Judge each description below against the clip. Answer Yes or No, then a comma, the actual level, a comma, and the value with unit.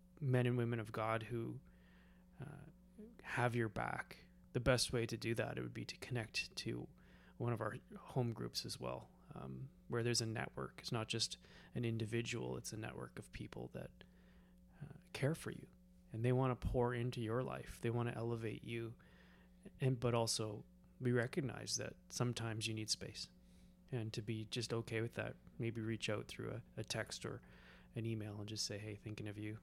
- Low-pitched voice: Yes, low, 115 Hz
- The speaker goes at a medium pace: Yes, average, 195 wpm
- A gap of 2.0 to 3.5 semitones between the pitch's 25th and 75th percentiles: Yes, average, 3.0 semitones